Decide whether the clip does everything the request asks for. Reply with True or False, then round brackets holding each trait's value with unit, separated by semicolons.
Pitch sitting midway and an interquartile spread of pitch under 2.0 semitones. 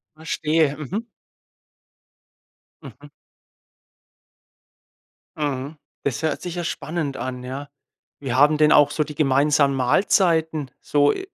False (150 Hz; 2.5 semitones)